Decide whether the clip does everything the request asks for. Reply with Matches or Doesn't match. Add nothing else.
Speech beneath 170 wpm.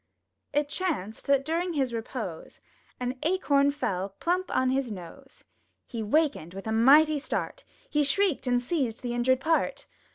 Matches